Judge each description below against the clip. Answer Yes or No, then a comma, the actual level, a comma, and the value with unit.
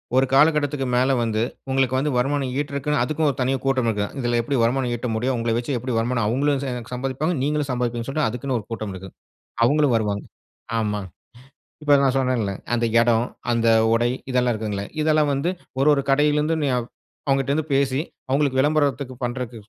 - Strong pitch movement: No, average, 3.2 semitones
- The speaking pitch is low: Yes, low, 130 Hz